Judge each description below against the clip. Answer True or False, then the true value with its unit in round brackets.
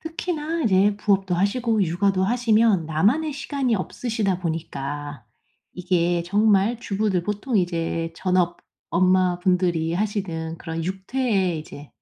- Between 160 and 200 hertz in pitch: True (190 Hz)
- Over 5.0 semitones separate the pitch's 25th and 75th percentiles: False (4.1 semitones)